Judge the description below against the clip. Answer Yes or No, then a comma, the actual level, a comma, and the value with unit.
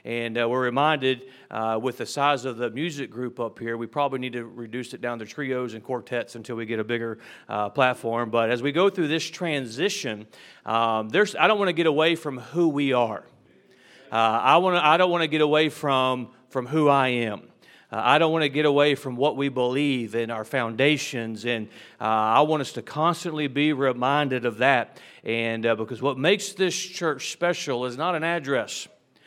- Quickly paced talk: Yes, fast, 210 wpm